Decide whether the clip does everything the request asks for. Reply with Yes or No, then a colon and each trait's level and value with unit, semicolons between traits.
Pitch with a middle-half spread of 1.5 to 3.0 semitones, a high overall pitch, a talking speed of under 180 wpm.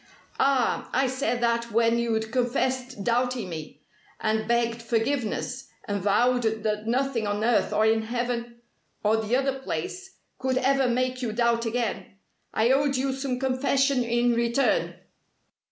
Yes: narrow, 2.6 semitones; high, 240 Hz; average, 145 wpm